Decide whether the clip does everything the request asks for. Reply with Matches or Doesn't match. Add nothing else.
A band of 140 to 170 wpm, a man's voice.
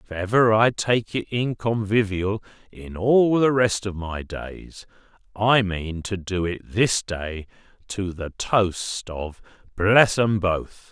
Matches